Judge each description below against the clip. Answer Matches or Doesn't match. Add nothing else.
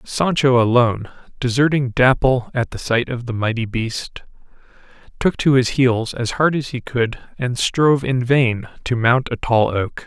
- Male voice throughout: Matches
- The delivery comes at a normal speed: Matches